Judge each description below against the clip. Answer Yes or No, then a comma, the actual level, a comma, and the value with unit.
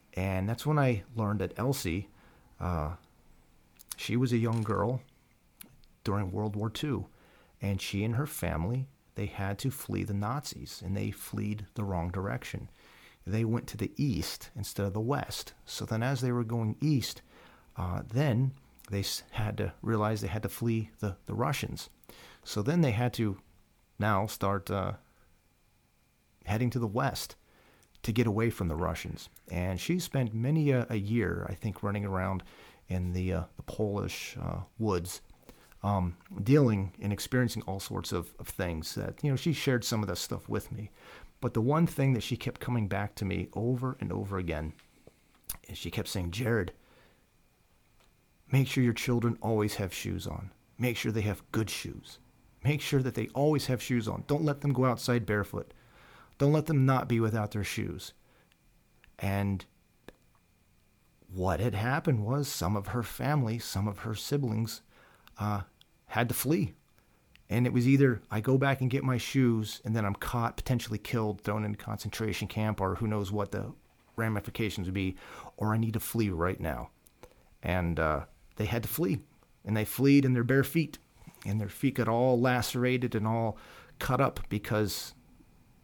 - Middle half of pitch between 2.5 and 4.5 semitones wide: Yes, average, 3.8 semitones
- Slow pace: No, average, 175 wpm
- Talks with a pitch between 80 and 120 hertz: Yes, low, 110 Hz